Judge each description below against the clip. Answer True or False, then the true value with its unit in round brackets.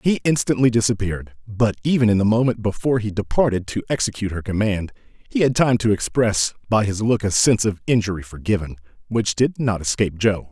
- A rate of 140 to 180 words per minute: False (190 wpm)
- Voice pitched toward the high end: False (105 Hz)